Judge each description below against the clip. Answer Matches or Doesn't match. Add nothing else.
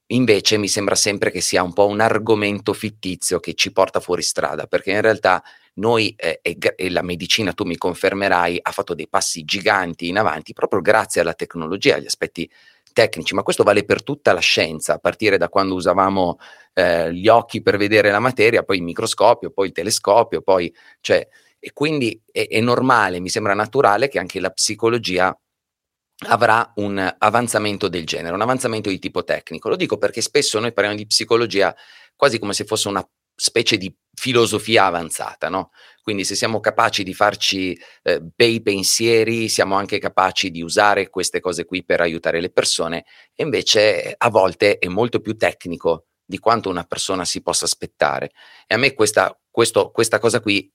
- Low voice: Matches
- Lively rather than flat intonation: Doesn't match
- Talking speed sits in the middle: Doesn't match